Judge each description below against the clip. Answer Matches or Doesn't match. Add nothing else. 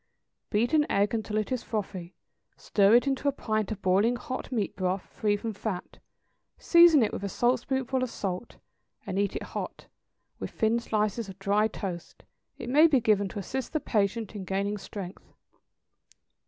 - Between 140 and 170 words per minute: Doesn't match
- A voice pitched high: Matches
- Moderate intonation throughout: Matches